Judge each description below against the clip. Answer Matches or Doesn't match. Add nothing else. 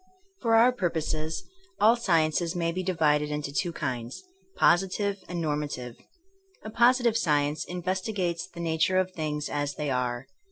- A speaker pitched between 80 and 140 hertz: Doesn't match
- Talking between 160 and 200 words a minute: Doesn't match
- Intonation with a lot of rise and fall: Doesn't match